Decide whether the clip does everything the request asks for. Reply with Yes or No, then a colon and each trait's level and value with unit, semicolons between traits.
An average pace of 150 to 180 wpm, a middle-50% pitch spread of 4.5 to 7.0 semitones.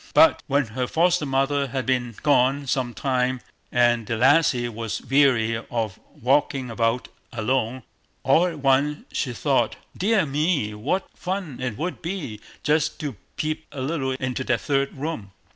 No: average, 155 wpm; average, 3.5 semitones